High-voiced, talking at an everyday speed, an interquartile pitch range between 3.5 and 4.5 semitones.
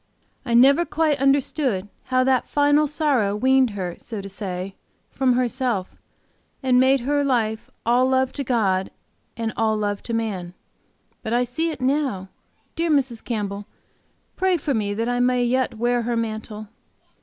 Yes: high, 245 Hz; average, 160 wpm; average, 3.8 semitones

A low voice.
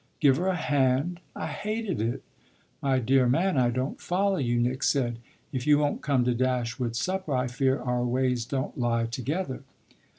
Yes: low, 130 Hz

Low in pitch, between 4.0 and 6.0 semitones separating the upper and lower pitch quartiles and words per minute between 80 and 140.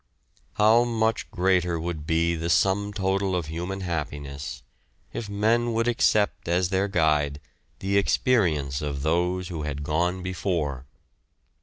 Yes: very low, 90 Hz; average, 4.5 semitones; slow, 135 wpm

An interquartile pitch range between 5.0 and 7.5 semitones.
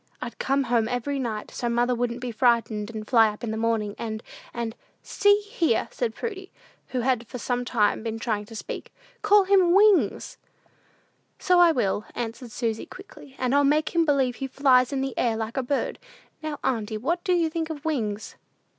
Yes: average, 5.3 semitones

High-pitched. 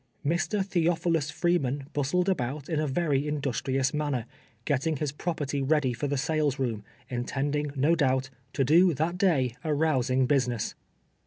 No: medium, 145 Hz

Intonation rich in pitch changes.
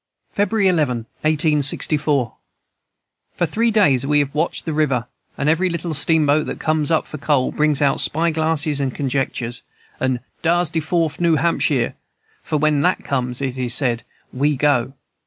No: average, 3.1 semitones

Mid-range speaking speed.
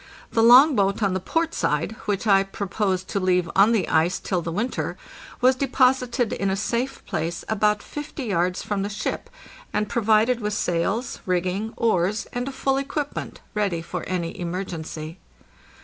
Yes: average, 170 wpm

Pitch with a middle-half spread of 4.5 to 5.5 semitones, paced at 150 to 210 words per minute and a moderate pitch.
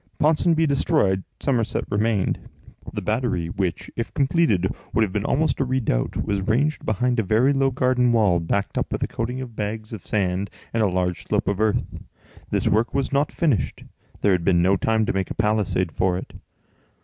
No: average, 5.1 semitones; average, 190 wpm; low, 110 Hz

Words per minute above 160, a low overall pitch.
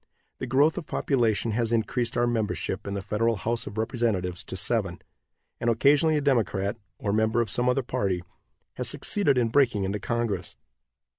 Yes: average, 170 wpm; low, 115 Hz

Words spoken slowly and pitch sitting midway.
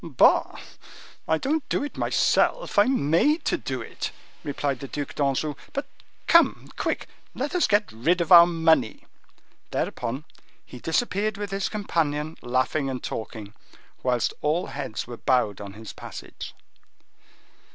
No: average, 145 wpm; medium, 150 Hz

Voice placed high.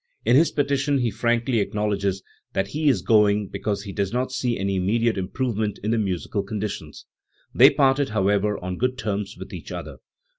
No: low, 105 Hz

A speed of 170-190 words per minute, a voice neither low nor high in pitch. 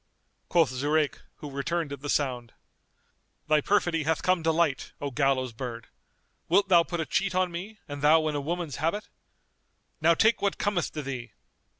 Yes: average, 180 wpm; medium, 155 Hz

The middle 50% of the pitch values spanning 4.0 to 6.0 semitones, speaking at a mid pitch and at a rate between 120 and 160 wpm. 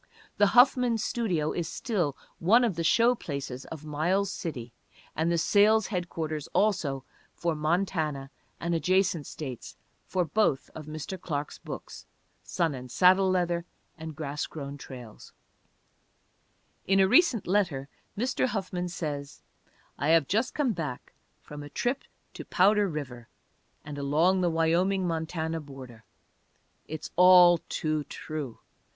Yes: average, 4.5 semitones; medium, 165 Hz; slow, 135 wpm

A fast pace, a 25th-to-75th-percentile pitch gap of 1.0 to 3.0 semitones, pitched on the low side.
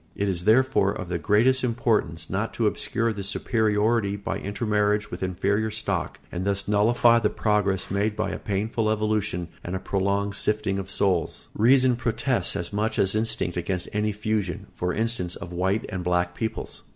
No: average, 175 wpm; narrow, 2.6 semitones; low, 105 Hz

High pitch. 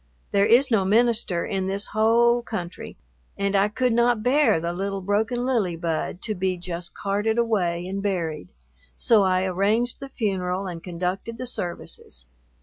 Yes: high, 200 Hz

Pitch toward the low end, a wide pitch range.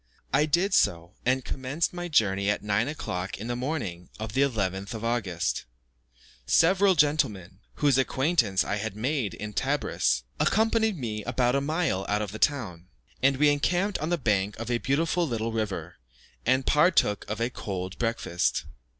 Yes: low, 120 Hz; wide, 6.5 semitones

